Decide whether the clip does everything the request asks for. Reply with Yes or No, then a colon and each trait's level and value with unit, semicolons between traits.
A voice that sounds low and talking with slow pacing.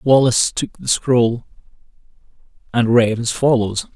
Yes: low, 120 Hz; slow, 120 wpm